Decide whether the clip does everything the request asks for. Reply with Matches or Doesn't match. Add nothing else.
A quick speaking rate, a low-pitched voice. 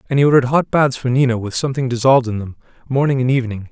Matches